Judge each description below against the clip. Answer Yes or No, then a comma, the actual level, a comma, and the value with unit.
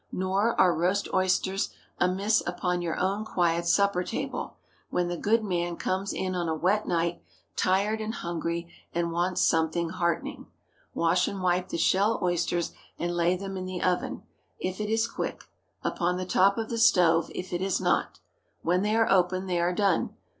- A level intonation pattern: Yes, narrow, 2.1 semitones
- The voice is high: No, medium, 180 Hz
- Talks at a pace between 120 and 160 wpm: No, average, 175 wpm